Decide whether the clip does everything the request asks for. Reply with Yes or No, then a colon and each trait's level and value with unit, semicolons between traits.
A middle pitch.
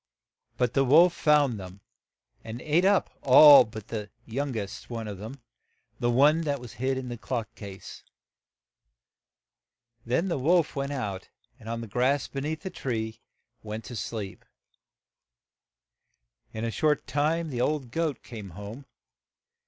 No: low, 125 Hz